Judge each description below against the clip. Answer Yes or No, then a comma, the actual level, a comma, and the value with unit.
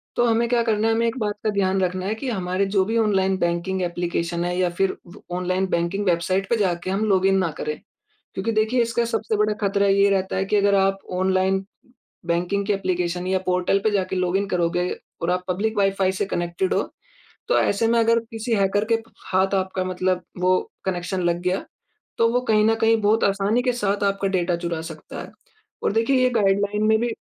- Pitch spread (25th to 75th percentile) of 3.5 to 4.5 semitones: No, narrow, 2.6 semitones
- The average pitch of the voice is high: Yes, high, 195 Hz